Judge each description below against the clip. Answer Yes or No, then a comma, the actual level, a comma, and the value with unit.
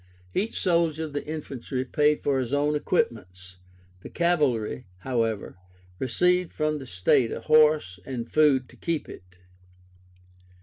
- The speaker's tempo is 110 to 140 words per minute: Yes, slow, 135 wpm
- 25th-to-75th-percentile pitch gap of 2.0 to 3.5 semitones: No, average, 5.1 semitones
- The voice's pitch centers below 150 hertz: Yes, medium, 140 Hz